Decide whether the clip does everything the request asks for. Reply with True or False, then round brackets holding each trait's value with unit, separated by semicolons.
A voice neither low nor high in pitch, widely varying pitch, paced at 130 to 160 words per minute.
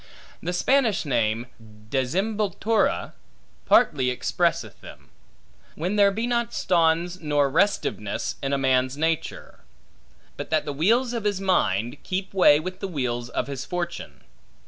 True (160 Hz; 6.8 semitones; 135 wpm)